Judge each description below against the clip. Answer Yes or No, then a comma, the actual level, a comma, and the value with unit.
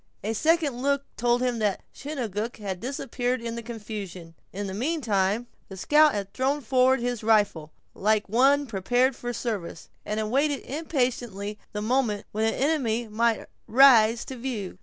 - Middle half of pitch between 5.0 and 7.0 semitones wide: No, average, 3.9 semitones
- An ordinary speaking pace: Yes, average, 160 wpm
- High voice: Yes, high, 235 Hz